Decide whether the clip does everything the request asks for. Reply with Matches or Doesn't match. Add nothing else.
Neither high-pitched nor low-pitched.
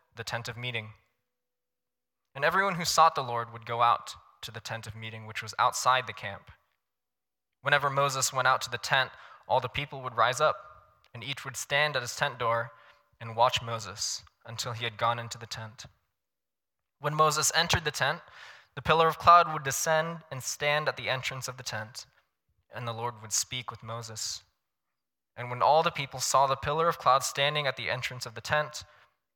Doesn't match